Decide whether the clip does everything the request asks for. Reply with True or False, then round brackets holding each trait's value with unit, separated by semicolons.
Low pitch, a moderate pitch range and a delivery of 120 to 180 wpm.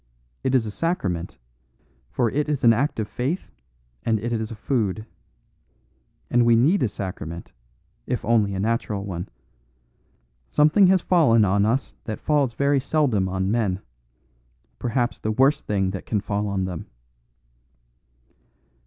True (115 Hz; 5.0 semitones; 145 wpm)